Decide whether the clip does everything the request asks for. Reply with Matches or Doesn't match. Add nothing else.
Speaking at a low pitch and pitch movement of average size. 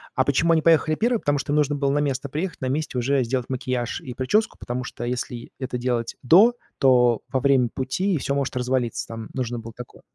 Matches